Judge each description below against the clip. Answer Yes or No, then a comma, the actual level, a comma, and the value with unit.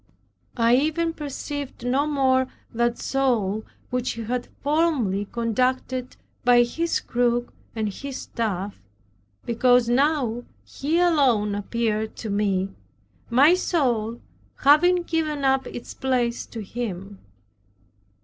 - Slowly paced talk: Yes, slow, 110 wpm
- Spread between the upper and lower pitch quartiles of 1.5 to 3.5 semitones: No, average, 3.9 semitones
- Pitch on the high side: Yes, high, 245 Hz